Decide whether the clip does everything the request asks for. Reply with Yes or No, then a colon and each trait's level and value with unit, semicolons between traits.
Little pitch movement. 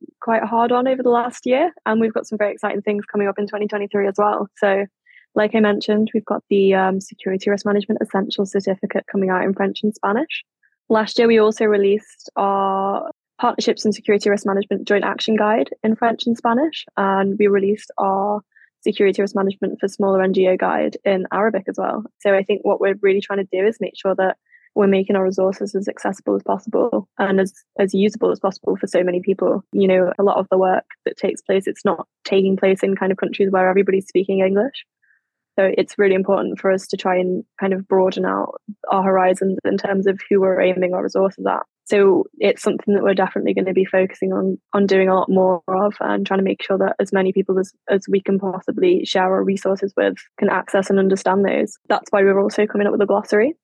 Yes: narrow, 1.6 semitones